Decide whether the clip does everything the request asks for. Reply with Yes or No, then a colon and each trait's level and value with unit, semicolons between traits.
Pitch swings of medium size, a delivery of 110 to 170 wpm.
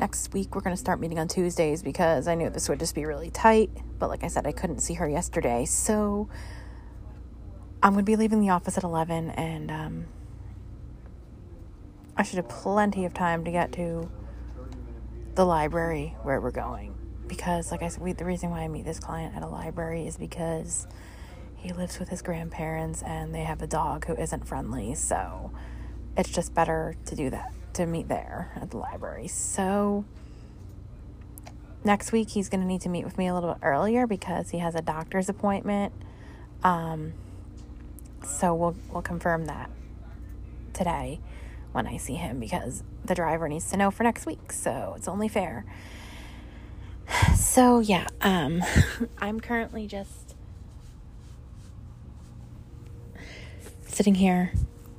No: wide, 6.0 semitones; average, 160 wpm